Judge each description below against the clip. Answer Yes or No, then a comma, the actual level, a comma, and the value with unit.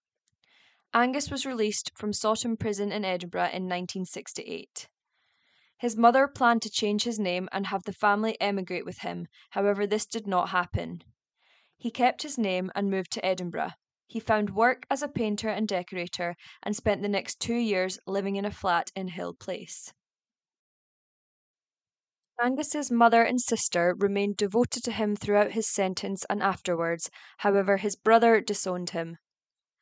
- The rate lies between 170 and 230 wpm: No, average, 155 wpm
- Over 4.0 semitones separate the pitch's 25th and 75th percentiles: No, average, 3.5 semitones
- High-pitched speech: Yes, high, 205 Hz